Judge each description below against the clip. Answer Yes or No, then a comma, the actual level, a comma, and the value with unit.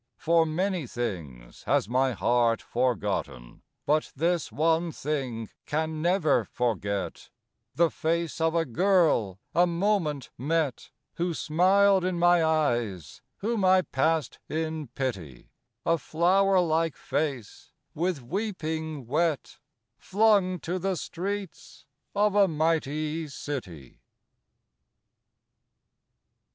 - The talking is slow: Yes, slow, 105 wpm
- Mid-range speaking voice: Yes, medium, 160 Hz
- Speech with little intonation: No, average, 5.3 semitones